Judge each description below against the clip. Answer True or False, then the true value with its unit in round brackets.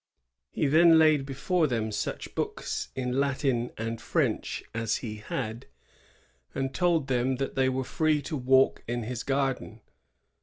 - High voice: False (130 Hz)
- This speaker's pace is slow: False (155 wpm)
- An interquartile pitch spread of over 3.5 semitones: False (2.9 semitones)